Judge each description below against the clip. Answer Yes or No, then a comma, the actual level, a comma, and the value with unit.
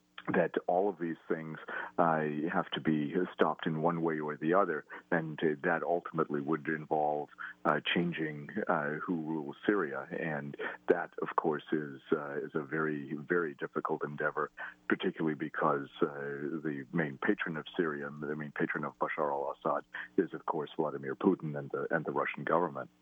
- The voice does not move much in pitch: Yes, narrow, 2.1 semitones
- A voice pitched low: Yes, very low, 75 Hz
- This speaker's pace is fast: No, average, 170 wpm